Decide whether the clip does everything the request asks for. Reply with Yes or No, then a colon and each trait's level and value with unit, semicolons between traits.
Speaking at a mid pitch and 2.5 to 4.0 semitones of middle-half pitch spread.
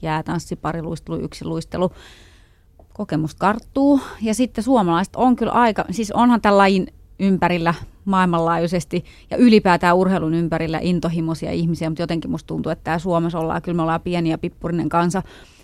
Yes: medium, 170 Hz; average, 2.9 semitones